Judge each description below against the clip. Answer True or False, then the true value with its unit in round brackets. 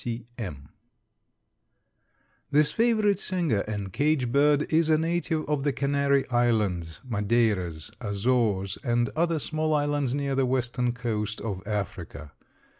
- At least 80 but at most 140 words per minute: True (135 wpm)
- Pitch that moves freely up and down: True (5.9 semitones)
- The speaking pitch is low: True (125 Hz)